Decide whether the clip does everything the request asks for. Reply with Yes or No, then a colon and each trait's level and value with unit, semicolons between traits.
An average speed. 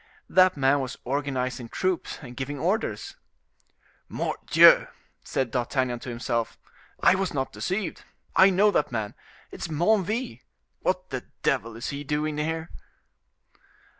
No: slow, 130 wpm